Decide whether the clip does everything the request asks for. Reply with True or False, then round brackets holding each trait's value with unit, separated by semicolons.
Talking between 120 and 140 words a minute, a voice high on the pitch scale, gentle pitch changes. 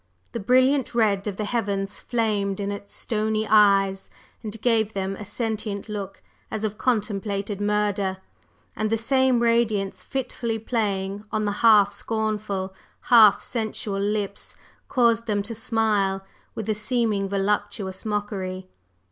True (135 wpm; 210 Hz; 2.0 semitones)